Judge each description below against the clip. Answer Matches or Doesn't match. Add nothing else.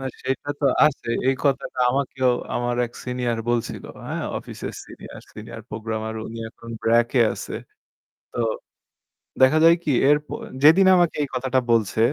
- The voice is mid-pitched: Doesn't match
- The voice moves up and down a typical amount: Matches